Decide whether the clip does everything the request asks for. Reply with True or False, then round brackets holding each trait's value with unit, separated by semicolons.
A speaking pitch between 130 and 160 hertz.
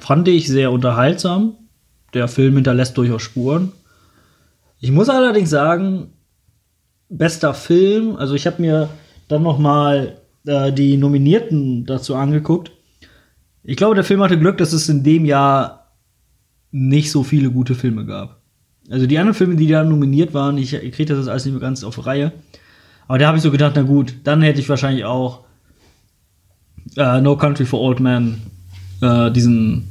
True (140 Hz)